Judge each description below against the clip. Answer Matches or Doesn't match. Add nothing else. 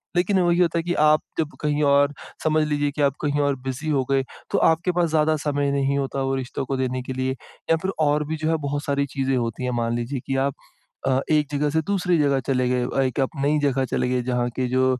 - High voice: Doesn't match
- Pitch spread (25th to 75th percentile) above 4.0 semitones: Doesn't match